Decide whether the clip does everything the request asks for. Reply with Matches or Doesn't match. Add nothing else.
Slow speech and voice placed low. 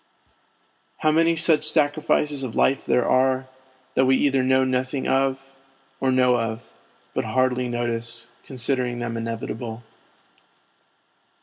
Matches